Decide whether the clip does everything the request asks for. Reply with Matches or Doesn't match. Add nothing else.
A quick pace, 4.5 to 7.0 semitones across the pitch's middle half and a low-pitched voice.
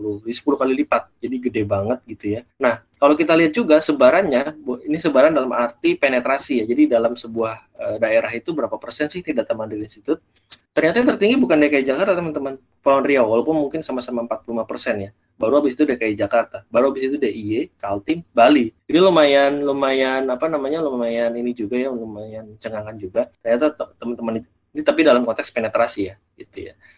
Matches